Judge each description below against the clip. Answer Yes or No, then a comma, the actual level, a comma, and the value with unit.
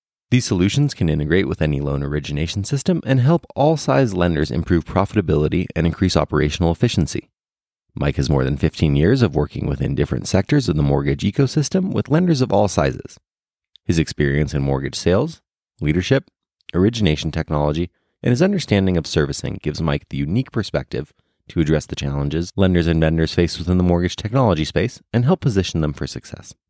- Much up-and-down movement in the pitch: Yes, wide, 7.7 semitones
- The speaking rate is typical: Yes, average, 175 wpm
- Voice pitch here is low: Yes, very low, 90 Hz